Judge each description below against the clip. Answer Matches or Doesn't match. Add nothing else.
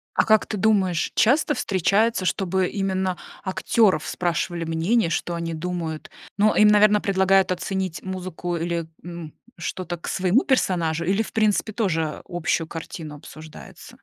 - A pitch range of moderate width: Matches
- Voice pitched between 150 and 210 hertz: Matches